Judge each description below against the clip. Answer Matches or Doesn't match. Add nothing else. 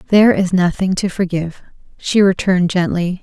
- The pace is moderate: Matches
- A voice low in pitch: Doesn't match